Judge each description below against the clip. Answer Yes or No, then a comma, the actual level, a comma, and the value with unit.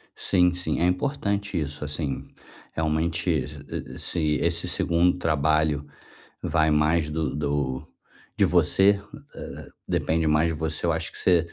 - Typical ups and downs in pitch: No, narrow, 2.3 semitones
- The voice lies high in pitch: No, very low, 80 Hz